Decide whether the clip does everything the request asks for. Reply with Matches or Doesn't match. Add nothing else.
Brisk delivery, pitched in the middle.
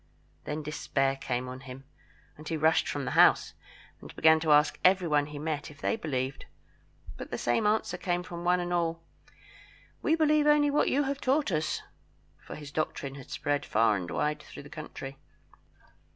Doesn't match